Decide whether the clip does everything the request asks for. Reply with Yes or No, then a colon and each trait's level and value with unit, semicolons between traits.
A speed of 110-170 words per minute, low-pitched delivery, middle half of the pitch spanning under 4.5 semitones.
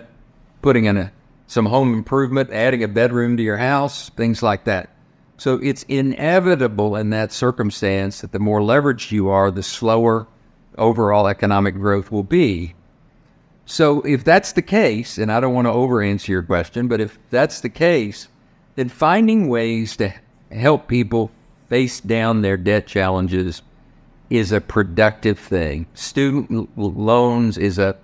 Yes: average, 155 wpm; low, 115 Hz; average, 4.1 semitones